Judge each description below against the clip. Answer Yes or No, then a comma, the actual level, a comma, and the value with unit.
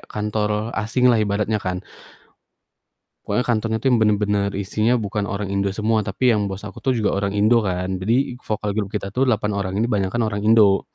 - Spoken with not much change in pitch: Yes, narrow, 2.0 semitones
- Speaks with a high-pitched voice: No, low, 105 Hz